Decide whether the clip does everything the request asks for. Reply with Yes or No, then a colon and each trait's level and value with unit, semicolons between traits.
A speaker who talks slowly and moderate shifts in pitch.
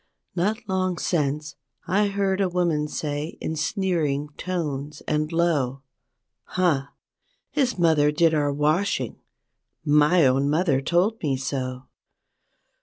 Yes: slow, 120 wpm; average, 4.0 semitones